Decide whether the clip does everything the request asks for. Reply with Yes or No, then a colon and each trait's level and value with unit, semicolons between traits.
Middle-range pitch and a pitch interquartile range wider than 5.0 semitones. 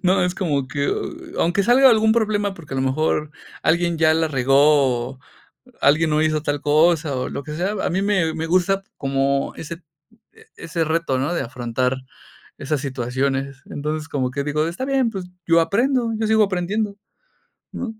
Yes: medium, 160 Hz; wide, 5.4 semitones